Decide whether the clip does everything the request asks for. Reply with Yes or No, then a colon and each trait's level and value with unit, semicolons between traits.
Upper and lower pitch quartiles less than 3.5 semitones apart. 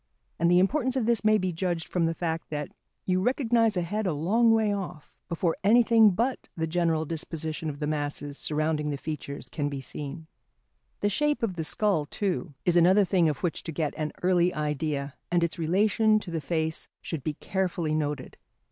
No: average, 4.6 semitones